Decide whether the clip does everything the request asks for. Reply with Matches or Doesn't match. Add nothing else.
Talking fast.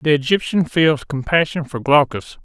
Doesn't match